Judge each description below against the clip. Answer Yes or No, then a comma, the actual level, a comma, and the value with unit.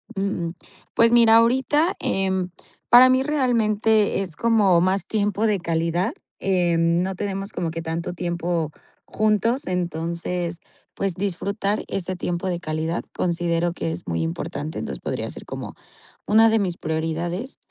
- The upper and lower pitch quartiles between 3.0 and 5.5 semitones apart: Yes, average, 4.1 semitones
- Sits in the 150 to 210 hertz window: Yes, medium, 185 Hz